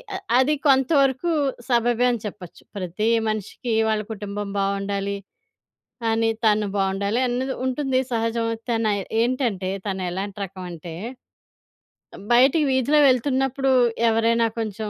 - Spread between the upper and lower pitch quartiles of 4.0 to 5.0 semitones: Yes, average, 4.4 semitones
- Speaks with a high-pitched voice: Yes, high, 225 Hz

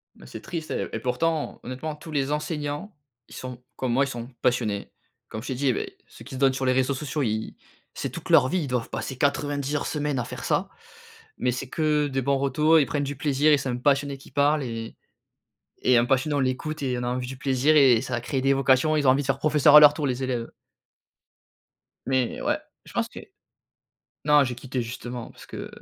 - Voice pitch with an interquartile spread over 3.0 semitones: No, average, 2.7 semitones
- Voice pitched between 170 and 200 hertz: No, low, 135 Hz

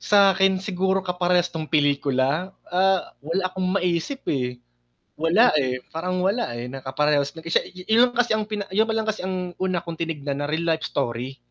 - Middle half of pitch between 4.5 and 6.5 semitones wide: Yes, average, 4.8 semitones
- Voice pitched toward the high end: No, medium, 175 Hz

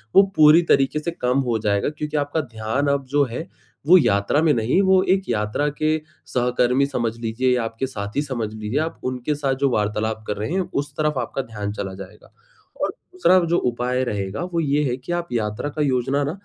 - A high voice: No, low, 130 Hz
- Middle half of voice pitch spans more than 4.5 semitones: Yes, average, 5.0 semitones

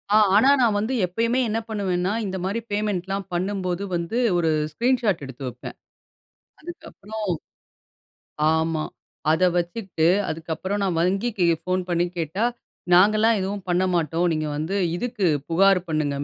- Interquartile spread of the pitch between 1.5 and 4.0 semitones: Yes, average, 3.7 semitones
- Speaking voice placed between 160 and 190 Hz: Yes, medium, 185 Hz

